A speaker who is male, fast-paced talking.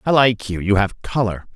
No: male; average, 195 wpm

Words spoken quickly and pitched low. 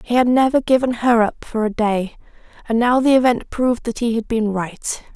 No: fast, 220 wpm; high, 235 Hz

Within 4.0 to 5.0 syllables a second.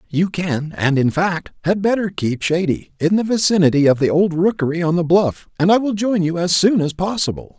No: 5.2 syllables/s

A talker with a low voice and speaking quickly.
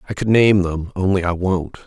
Yes: very low, 95 Hz; fast, 225 wpm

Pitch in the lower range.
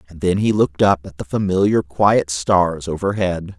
Yes: very low, 90 Hz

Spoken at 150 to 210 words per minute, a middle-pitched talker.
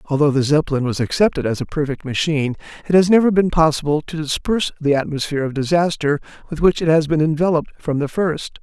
Yes: average, 200 wpm; medium, 155 Hz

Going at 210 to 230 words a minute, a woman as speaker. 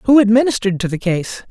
No: average, 200 wpm; female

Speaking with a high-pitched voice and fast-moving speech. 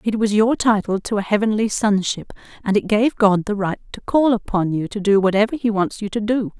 Yes: high, 210 Hz; fast, 235 wpm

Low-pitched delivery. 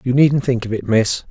Yes: low, 125 Hz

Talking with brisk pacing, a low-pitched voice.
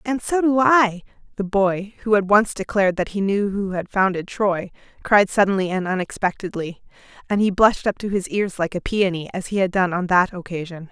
No: fast, 210 wpm; high, 195 Hz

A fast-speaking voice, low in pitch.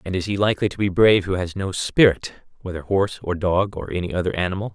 Yes: fast, 240 wpm; very low, 95 Hz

